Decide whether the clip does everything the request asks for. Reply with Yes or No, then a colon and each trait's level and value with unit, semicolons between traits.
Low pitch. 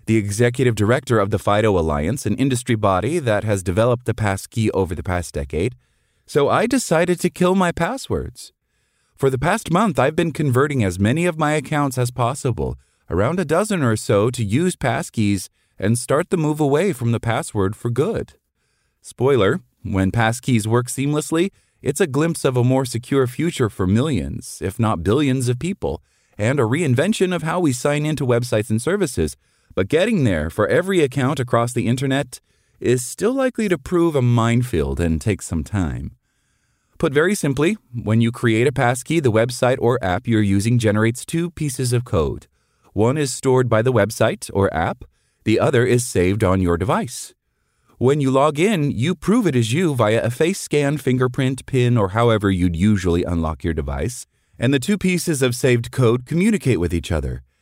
Yes: low, 120 Hz